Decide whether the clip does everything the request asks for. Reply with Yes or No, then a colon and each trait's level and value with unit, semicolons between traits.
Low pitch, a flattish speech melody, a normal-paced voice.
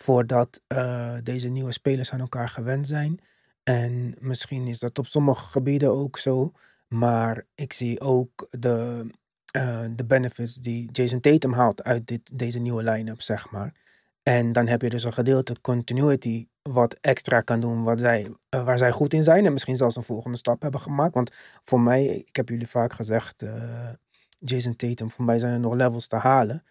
Yes: low, 125 Hz; narrow, 1.9 semitones; average, 190 wpm